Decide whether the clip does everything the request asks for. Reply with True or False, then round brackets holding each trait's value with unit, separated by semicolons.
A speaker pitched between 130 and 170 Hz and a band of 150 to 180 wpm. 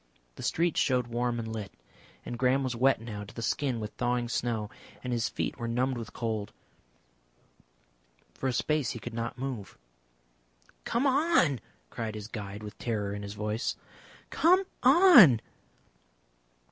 False (120 Hz; 155 wpm)